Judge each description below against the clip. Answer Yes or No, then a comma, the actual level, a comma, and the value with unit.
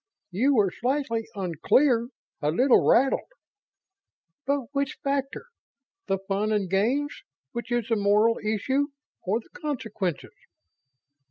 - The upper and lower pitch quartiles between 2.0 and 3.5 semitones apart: No, average, 5.1 semitones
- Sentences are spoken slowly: Yes, slow, 115 wpm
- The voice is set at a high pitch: Yes, high, 230 Hz